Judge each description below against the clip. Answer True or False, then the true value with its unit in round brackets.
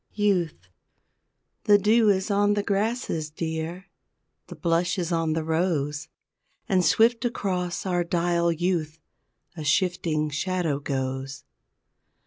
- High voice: False (175 Hz)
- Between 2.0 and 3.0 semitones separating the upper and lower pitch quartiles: False (3.7 semitones)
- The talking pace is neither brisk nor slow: False (115 wpm)